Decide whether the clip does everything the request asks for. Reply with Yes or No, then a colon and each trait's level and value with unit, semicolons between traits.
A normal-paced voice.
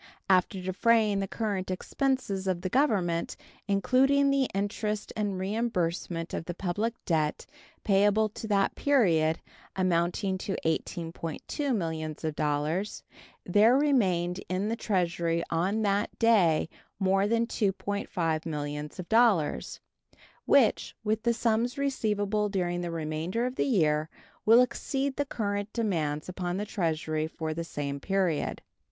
No: slow, 125 wpm